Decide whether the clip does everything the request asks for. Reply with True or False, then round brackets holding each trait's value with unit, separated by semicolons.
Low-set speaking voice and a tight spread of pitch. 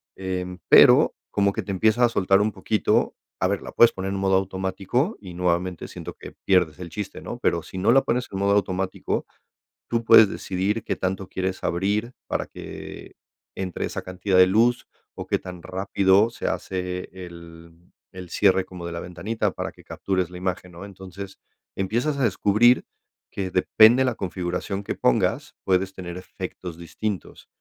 True (95 Hz; 2.2 semitones)